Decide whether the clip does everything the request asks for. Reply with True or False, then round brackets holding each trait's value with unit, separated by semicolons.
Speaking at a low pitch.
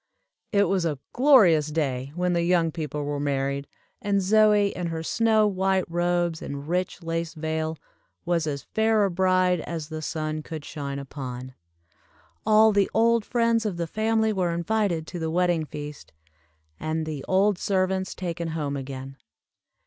False (170 Hz)